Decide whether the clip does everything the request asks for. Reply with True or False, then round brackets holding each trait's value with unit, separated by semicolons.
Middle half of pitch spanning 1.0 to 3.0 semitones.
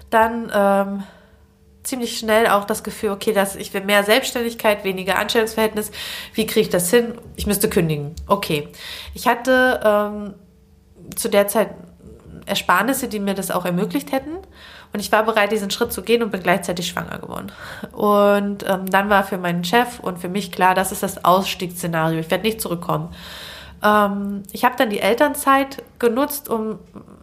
True (2.7 semitones)